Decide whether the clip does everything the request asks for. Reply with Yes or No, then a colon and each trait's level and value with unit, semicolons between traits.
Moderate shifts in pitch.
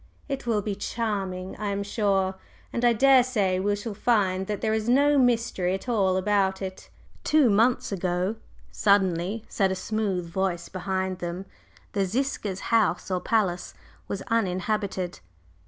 Yes: average, 3.1 semitones